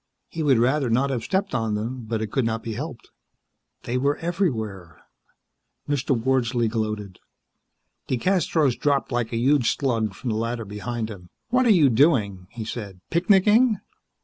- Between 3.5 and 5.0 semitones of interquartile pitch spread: Yes, average, 4.7 semitones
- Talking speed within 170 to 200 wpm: No, average, 160 wpm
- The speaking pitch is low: Yes, low, 120 Hz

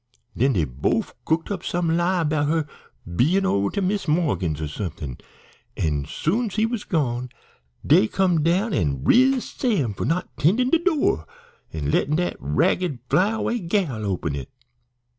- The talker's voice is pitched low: No, medium, 160 Hz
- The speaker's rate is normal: Yes, average, 170 wpm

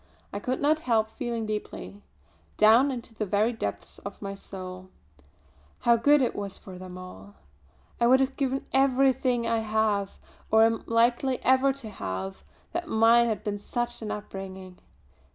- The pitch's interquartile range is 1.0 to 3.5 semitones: No, average, 4.1 semitones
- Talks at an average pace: Yes, average, 160 wpm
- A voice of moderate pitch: No, high, 225 Hz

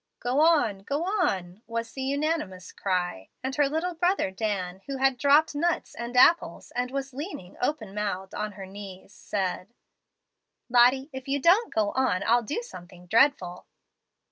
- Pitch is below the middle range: No, high, 245 Hz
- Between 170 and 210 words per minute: No, average, 160 wpm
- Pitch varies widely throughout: Yes, wide, 7.0 semitones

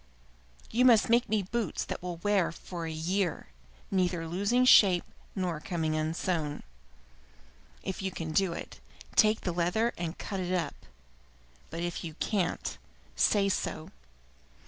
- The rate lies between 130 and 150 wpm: Yes, average, 145 wpm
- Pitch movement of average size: Yes, average, 3.4 semitones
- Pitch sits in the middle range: Yes, medium, 180 Hz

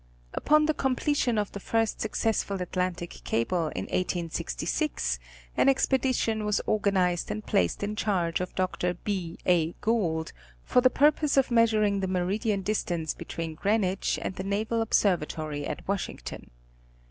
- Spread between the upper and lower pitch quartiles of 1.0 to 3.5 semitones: No, average, 4.2 semitones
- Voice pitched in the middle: No, high, 195 Hz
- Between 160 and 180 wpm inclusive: No, average, 140 wpm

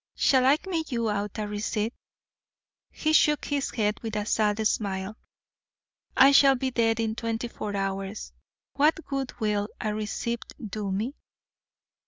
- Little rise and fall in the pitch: No, average, 4.1 semitones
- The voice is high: Yes, high, 220 Hz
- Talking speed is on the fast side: No, average, 150 wpm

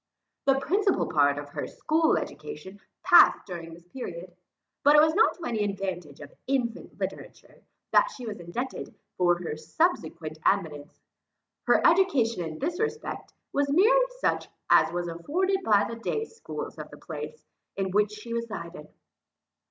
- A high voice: Yes, high, 215 Hz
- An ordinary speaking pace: Yes, average, 155 wpm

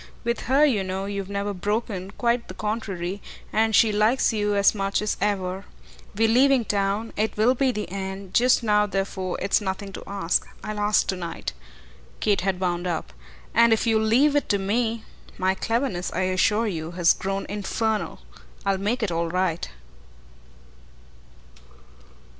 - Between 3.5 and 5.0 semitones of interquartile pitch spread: No, average, 2.8 semitones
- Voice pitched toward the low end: No, high, 205 Hz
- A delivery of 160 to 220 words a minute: Yes, average, 165 wpm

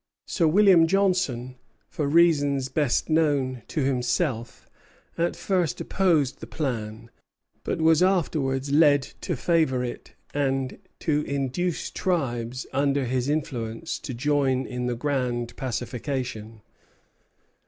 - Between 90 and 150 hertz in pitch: Yes, medium, 140 Hz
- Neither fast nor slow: No, slow, 115 wpm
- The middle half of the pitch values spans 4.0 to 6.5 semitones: Yes, average, 4.3 semitones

